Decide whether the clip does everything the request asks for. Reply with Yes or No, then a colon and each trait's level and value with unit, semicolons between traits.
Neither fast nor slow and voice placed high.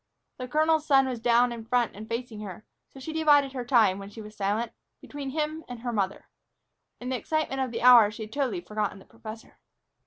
No: fast, 215 wpm; high, 240 Hz